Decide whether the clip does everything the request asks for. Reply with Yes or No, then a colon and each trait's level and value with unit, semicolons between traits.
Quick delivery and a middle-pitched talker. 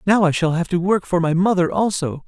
Yes: fast, 265 wpm; medium, 180 Hz